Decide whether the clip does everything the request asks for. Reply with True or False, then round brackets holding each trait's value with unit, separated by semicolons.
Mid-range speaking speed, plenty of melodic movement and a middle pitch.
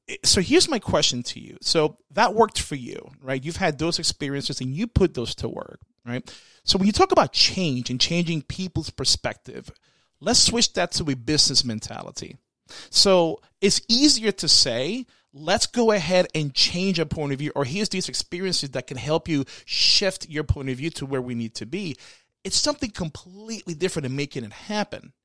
True (195 wpm; 6.1 semitones; 165 Hz)